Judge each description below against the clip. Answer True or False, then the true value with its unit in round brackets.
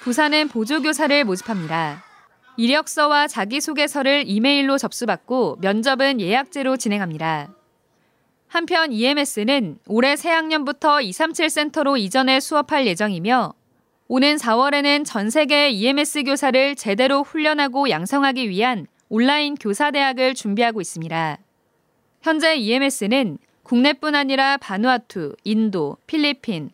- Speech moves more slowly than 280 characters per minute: False (300 characters per minute)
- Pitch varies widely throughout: False (4.8 semitones)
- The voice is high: True (270 Hz)